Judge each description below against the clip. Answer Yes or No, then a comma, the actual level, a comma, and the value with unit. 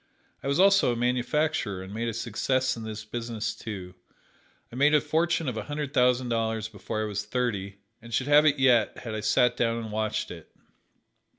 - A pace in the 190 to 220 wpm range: Yes, average, 200 wpm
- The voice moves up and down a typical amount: Yes, average, 3.7 semitones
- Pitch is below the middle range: Yes, low, 115 Hz